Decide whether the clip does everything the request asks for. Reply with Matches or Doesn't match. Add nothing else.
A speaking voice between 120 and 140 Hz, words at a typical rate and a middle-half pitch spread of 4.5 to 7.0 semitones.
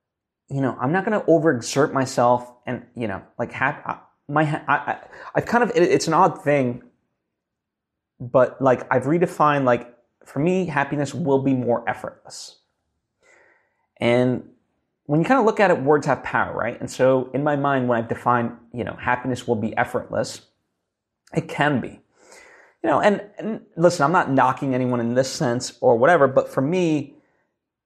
Matches